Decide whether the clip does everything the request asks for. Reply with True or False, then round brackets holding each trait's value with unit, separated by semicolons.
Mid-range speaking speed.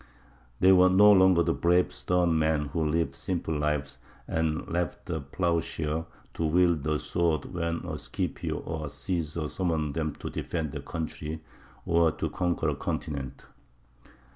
True (155 wpm)